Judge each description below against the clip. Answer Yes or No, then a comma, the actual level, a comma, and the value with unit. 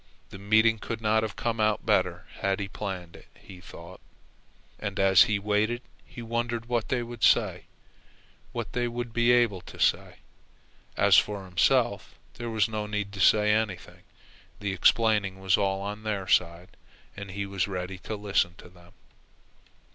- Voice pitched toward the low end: Yes, low, 105 Hz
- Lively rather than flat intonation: No, narrow, 2.6 semitones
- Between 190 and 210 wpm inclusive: No, average, 170 wpm